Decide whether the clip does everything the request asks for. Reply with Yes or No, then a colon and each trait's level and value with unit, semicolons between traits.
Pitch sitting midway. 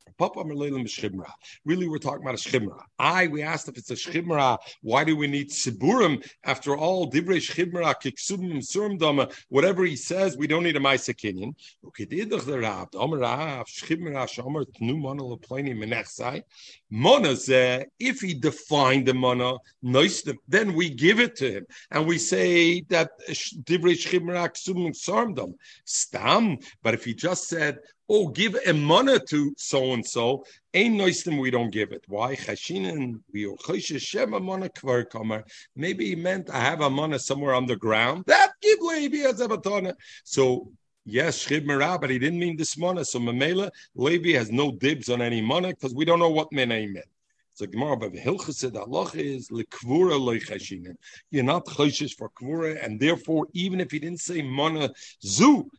Yes: medium, 150 Hz